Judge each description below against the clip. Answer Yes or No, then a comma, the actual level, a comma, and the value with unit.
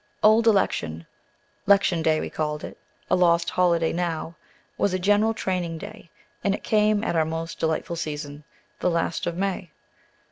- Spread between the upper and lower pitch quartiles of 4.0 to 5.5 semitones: No, average, 3.4 semitones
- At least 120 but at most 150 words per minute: No, average, 165 wpm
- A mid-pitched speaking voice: Yes, medium, 170 Hz